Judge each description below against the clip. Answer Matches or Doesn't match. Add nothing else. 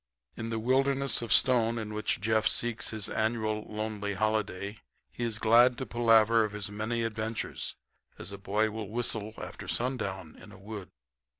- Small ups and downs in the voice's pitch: Matches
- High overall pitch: Doesn't match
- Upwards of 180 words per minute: Doesn't match